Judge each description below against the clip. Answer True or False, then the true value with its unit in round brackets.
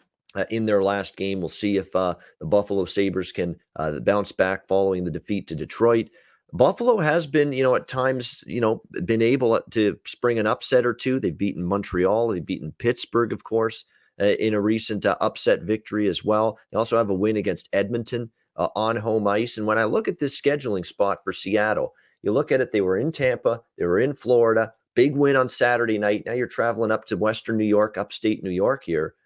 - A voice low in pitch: True (110 Hz)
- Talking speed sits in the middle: False (215 wpm)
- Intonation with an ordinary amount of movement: True (3.0 semitones)